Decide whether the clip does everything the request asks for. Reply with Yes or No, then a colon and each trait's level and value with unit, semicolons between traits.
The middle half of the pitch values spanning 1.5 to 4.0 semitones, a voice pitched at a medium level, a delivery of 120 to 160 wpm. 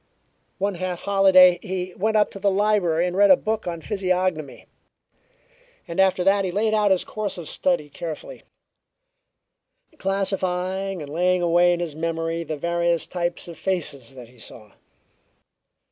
Yes: narrow, 2.6 semitones; medium, 180 Hz; average, 155 wpm